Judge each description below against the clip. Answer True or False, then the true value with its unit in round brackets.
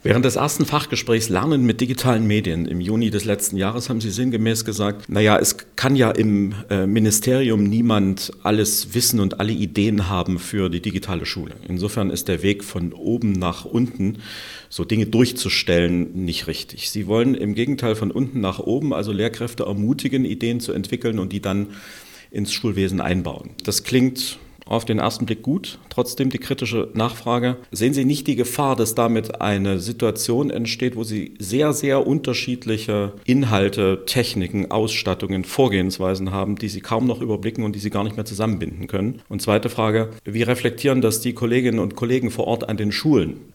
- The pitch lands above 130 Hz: False (110 Hz)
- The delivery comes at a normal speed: True (175 wpm)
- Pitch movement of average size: True (3.5 semitones)